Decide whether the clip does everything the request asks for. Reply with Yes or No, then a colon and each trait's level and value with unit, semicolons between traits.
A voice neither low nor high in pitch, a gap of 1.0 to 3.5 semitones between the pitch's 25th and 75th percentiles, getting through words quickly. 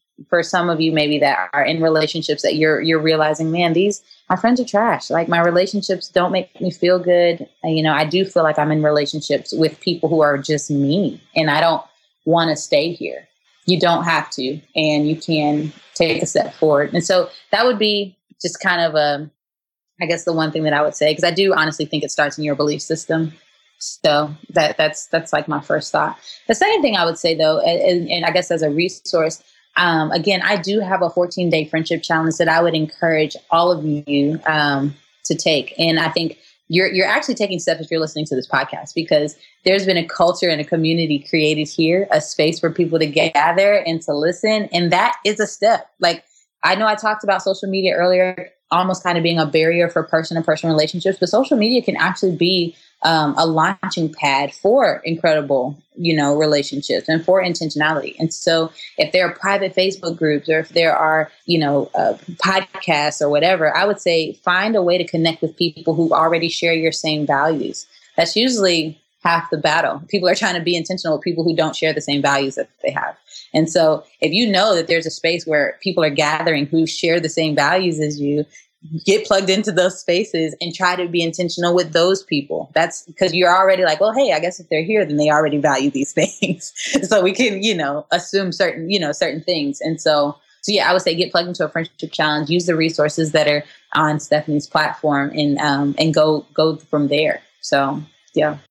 Yes: medium, 165 Hz; average, 2.8 semitones; fast, 215 wpm